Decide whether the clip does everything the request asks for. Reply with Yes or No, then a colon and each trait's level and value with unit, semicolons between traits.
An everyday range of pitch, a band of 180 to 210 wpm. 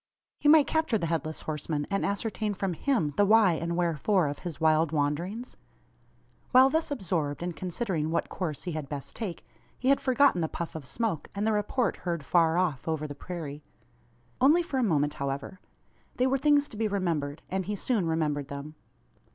No: wide, 6.2 semitones; average, 190 wpm